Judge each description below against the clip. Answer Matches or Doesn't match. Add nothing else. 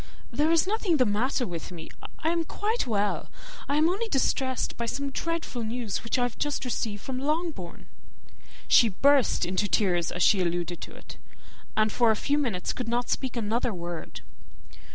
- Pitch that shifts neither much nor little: Doesn't match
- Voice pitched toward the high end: Matches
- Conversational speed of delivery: Matches